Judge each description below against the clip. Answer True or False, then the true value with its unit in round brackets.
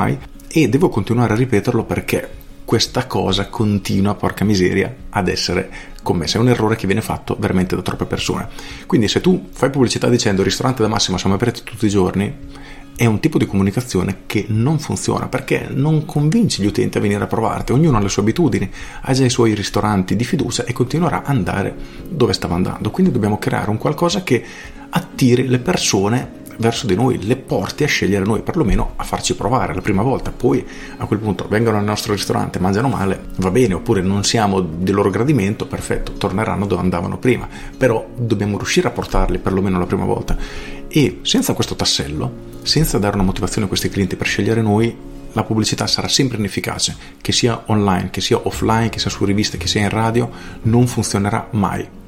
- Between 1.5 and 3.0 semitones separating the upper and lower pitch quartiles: False (4.0 semitones)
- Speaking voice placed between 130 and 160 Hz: False (105 Hz)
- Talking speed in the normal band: False (190 wpm)